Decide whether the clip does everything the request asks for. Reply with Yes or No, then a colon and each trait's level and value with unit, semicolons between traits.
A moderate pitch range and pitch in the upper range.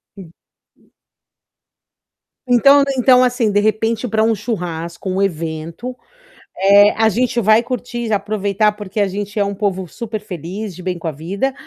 Yes: average, 3.7 semitones; high, 210 Hz